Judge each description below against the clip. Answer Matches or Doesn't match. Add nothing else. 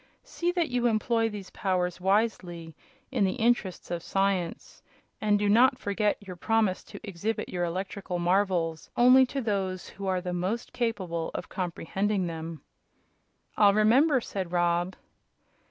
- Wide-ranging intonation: Doesn't match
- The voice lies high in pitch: Matches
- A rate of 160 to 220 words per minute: Doesn't match